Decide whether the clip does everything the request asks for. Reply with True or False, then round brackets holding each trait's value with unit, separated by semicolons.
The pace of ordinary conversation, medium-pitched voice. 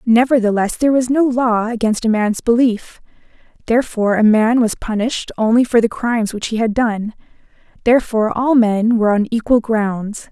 False (170 wpm; 230 Hz)